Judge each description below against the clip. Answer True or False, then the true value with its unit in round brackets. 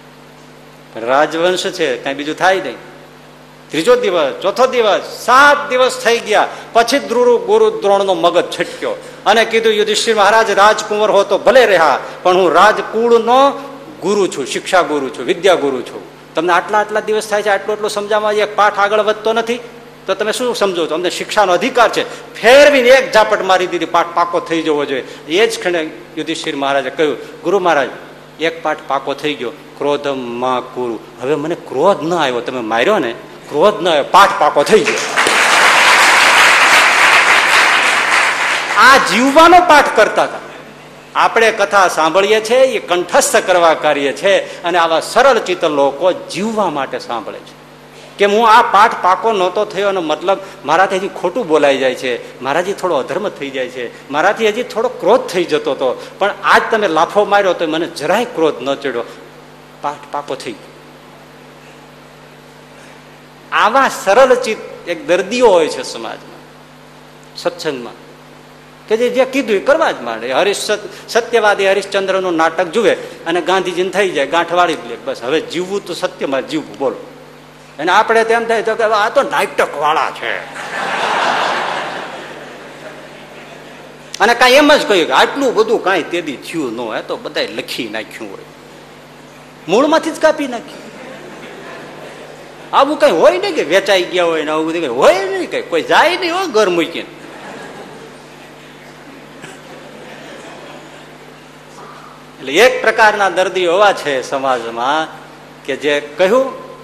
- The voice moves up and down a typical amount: False (6.9 semitones)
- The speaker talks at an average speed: False (150 wpm)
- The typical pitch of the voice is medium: False (200 Hz)